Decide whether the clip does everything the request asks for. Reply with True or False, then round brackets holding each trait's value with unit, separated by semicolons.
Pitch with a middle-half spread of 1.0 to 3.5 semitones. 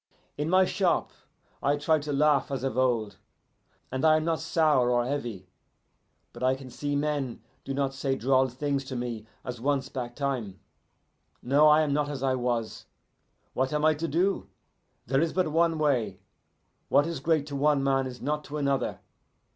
True (2.9 semitones)